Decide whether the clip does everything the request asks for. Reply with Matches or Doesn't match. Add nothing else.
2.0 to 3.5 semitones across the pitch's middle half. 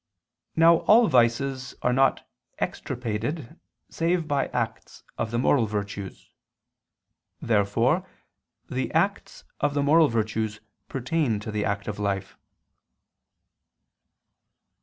Doesn't match